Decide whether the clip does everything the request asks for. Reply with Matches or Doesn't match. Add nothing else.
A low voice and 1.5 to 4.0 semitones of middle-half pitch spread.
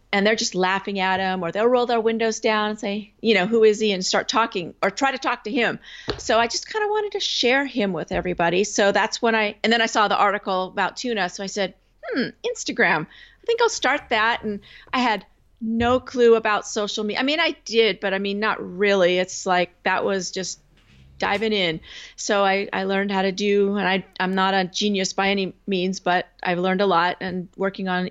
Doesn't match